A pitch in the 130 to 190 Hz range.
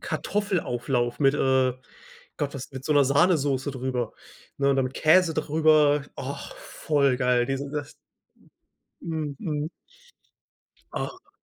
Yes: medium, 140 Hz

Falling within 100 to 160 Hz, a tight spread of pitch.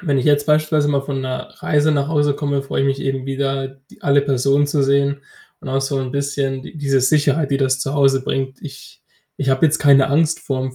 Yes: medium, 140 Hz; narrow, 1.3 semitones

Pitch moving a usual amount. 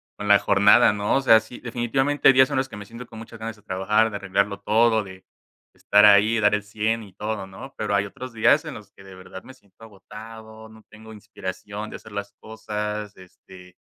No: narrow, 1.8 semitones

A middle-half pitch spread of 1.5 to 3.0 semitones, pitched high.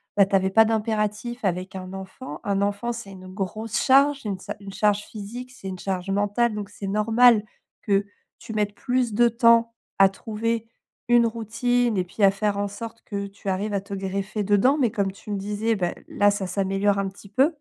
Yes: average, 2.7 semitones; high, 205 Hz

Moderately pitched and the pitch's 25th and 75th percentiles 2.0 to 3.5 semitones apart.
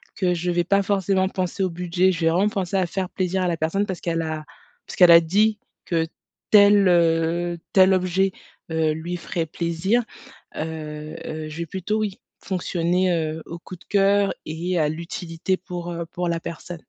Yes: medium, 175 Hz; narrow, 2.4 semitones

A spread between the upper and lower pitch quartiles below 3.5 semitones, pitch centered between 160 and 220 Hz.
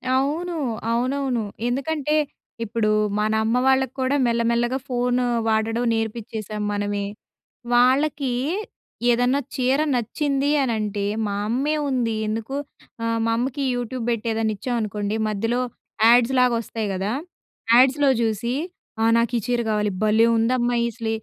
No: average, 2.8 semitones; high, 235 Hz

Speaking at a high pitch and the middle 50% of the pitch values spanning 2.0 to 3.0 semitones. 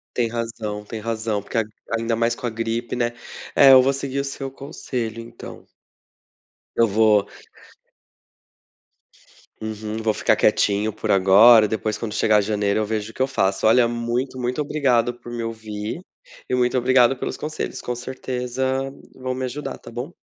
No: low, 115 Hz; average, 2.7 semitones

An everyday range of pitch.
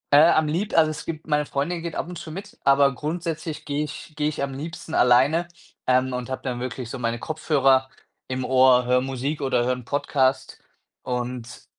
Yes: average, 3.4 semitones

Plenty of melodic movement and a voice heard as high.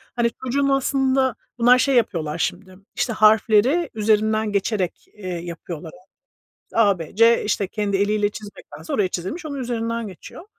No: average, 4.1 semitones; high, 215 Hz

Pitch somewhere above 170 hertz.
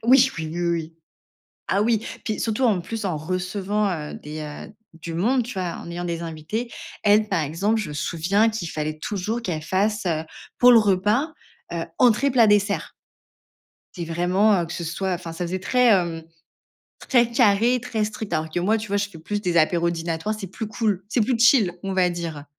Yes: high, 190 Hz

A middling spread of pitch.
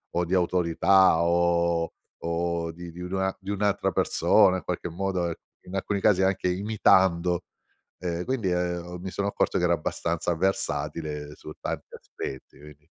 No: narrow, 2.1 semitones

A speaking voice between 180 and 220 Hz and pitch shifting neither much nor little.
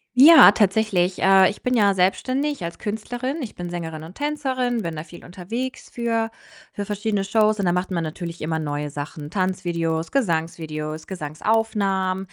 Yes: high, 190 Hz; average, 5.0 semitones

